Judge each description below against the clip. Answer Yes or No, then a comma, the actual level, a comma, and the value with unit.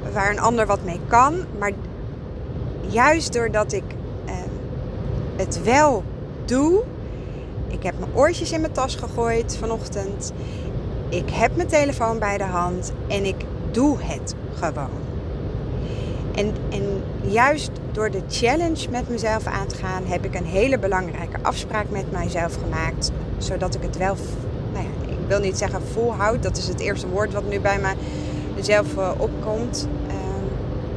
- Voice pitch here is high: Yes, high, 205 Hz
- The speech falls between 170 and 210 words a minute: No, average, 150 wpm